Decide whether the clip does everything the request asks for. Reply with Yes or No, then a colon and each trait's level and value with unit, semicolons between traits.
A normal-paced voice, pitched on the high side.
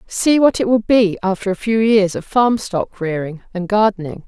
No: fast, 210 wpm; high, 205 Hz